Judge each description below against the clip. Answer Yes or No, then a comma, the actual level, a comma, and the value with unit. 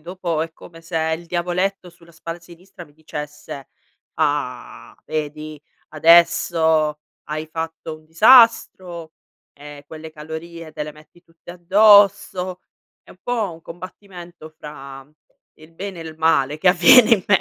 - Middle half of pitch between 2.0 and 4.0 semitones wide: Yes, narrow, 2.5 semitones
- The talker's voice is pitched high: No, medium, 165 Hz